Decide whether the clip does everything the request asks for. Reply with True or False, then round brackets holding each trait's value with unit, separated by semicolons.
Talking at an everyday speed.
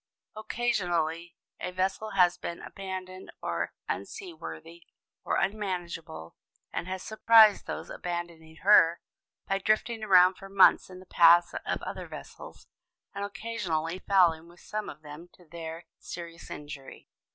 False (130 wpm)